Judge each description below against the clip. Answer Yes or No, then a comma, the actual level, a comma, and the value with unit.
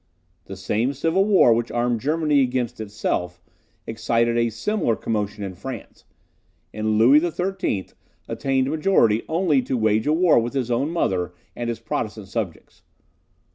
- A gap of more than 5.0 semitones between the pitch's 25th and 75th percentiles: Yes, wide, 5.4 semitones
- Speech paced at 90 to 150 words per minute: Yes, average, 145 wpm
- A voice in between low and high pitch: No, low, 120 Hz